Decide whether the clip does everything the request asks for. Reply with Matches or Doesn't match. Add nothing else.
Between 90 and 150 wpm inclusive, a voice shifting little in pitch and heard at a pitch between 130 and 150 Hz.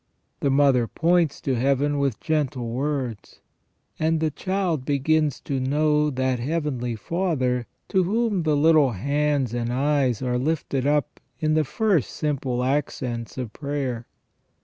Doesn't match